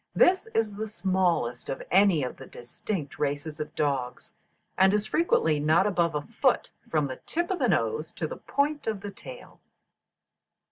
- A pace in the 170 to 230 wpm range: Yes, average, 175 wpm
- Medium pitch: Yes, medium, 175 Hz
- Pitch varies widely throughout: Yes, wide, 6.3 semitones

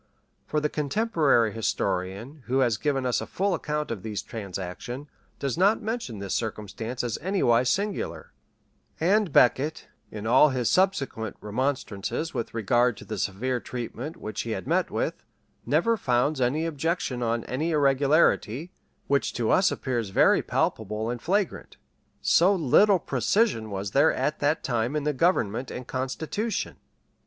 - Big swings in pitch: Yes, wide, 5.9 semitones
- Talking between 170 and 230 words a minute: No, average, 150 wpm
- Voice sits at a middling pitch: No, low, 130 Hz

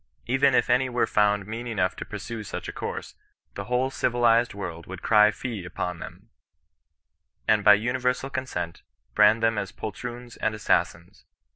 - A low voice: Yes, low, 115 Hz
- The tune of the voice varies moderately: Yes, average, 3.2 semitones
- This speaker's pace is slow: No, average, 165 wpm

